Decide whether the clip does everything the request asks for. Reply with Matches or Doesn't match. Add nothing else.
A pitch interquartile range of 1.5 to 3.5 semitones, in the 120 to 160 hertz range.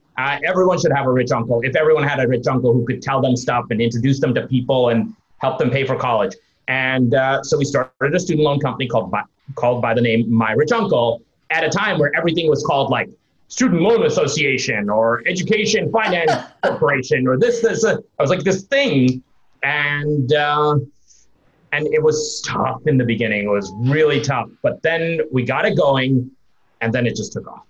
Doesn't match